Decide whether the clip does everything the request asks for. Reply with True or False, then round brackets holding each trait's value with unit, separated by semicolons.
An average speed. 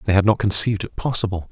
False (235 wpm)